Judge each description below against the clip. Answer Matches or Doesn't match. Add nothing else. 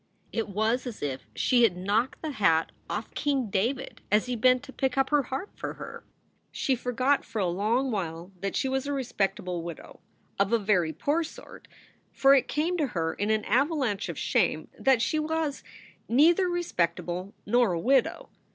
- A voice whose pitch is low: Doesn't match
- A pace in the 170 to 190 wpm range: Matches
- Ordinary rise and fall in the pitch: Doesn't match